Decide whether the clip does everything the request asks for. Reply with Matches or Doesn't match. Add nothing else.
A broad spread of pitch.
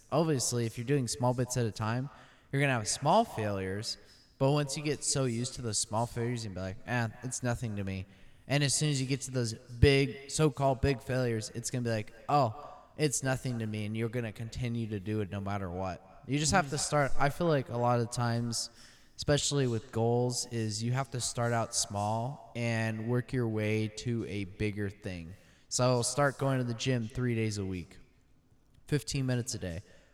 Doesn't match